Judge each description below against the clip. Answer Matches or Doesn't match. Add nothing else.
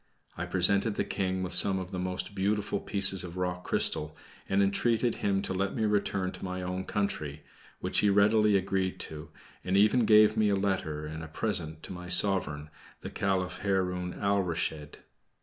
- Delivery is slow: Doesn't match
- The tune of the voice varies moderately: Doesn't match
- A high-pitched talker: Doesn't match